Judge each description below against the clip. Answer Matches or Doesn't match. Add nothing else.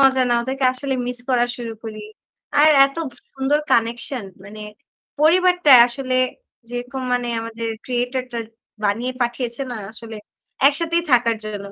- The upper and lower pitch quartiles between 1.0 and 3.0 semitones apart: Matches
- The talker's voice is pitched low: Doesn't match